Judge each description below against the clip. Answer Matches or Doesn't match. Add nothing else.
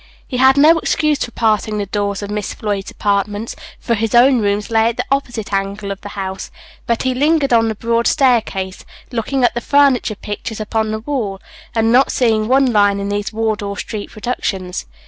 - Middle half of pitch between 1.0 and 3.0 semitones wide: Doesn't match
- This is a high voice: Matches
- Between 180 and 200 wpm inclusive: Matches